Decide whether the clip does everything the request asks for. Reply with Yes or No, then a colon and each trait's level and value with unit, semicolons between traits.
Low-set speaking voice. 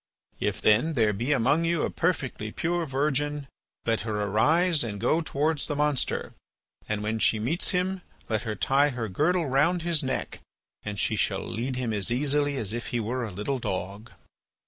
Yes: low, 130 Hz